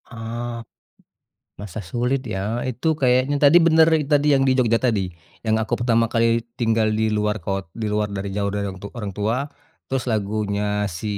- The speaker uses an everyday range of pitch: Yes, average, 3.2 semitones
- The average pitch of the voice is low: Yes, low, 115 Hz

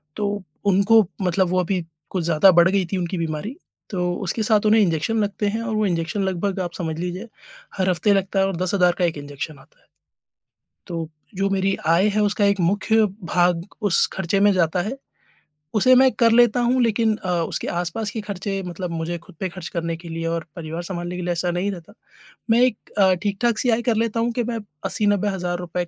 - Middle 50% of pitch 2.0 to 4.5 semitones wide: Yes, average, 3.3 semitones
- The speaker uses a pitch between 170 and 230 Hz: Yes, high, 190 Hz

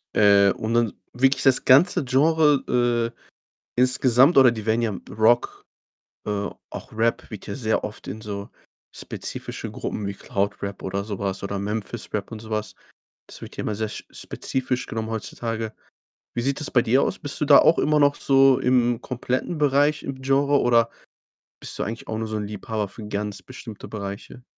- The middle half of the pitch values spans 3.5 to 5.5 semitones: Yes, average, 3.9 semitones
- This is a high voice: No, low, 115 Hz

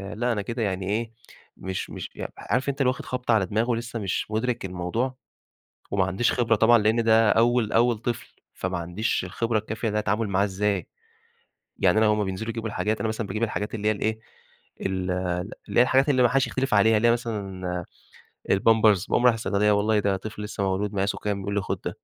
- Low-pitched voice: Yes, low, 110 Hz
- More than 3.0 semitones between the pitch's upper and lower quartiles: No, average, 2.7 semitones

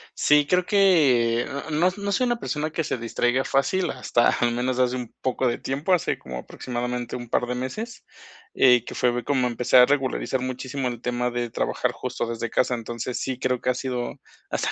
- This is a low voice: Yes, low, 125 Hz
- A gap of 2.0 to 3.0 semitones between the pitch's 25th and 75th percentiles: Yes, average, 2.7 semitones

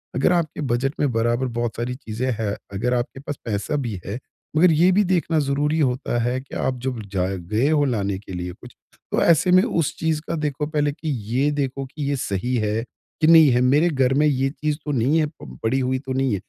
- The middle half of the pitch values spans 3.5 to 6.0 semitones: Yes, average, 4.0 semitones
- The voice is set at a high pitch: No, low, 130 Hz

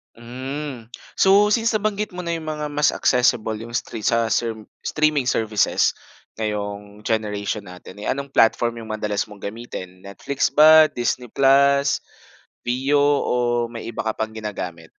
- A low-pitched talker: Yes, low, 120 Hz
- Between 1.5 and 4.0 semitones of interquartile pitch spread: No, average, 4.9 semitones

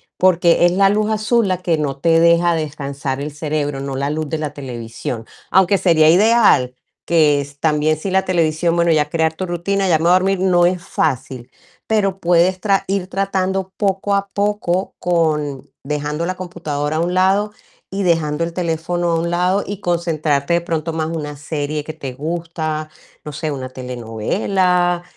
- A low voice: No, medium, 165 Hz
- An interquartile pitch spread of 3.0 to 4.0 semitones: Yes, average, 3.7 semitones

